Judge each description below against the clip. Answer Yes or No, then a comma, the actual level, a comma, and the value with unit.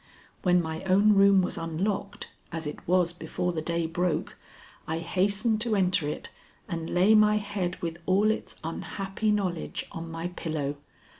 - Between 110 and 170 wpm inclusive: Yes, average, 160 wpm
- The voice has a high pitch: No, medium, 180 Hz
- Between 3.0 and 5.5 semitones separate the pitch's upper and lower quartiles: Yes, average, 3.5 semitones